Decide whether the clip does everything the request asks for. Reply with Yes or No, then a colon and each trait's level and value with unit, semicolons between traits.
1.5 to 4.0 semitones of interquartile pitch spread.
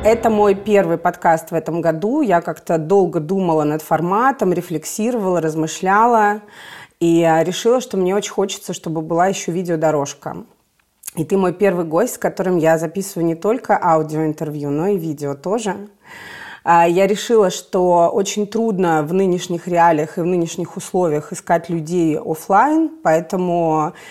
Yes: average, 3.4 semitones